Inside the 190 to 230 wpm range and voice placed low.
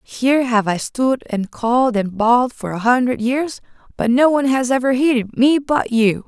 No: average, 200 wpm; high, 245 Hz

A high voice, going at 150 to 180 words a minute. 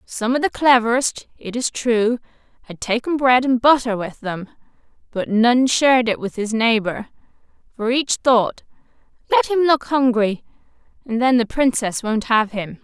Yes: high, 240 Hz; average, 165 wpm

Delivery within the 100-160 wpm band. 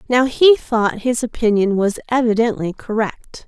Yes: average, 140 wpm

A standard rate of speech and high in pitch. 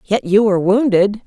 Yes: average, 190 wpm; high, 205 Hz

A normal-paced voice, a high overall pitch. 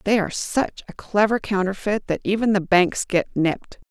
Yes: average, 185 wpm; high, 195 Hz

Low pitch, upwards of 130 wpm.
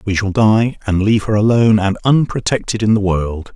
Yes: low, 105 Hz; fast, 205 wpm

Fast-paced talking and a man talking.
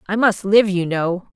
No: fast, 220 wpm; female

